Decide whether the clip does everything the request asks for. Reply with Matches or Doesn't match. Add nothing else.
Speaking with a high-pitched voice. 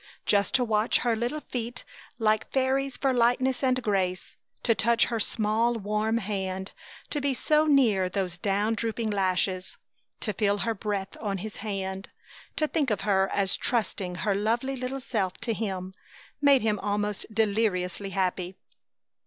Matches